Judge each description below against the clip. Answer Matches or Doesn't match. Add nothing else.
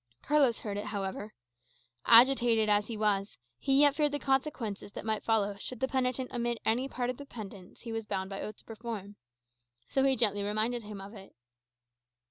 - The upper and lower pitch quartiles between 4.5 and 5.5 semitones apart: Doesn't match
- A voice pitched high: Matches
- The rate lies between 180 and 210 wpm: Matches